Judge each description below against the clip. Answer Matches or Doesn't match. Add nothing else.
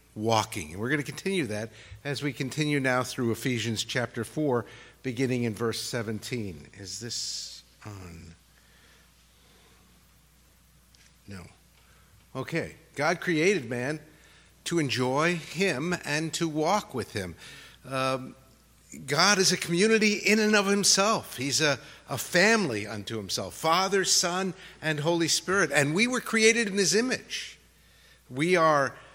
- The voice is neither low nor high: Matches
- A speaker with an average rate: Doesn't match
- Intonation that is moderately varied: Doesn't match